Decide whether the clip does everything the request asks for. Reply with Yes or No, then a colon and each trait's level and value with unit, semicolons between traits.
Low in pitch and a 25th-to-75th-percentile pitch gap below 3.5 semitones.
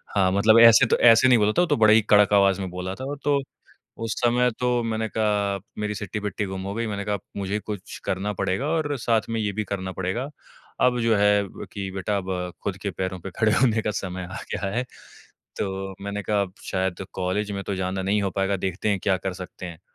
Yes: low, 100 Hz; average, 2.7 semitones